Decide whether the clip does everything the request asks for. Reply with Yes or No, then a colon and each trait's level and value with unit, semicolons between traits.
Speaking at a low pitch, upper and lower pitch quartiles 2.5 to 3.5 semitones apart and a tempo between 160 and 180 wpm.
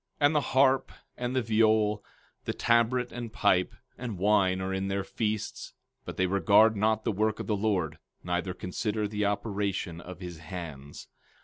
Yes: low, 105 Hz; average, 3.0 semitones; average, 175 wpm